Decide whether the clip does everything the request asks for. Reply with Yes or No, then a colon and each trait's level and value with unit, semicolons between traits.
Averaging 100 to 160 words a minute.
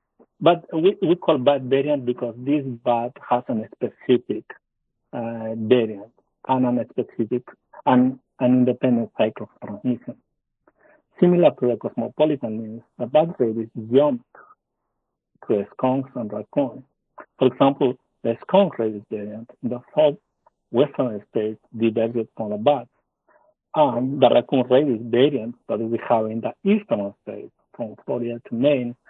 Yes: average, 140 wpm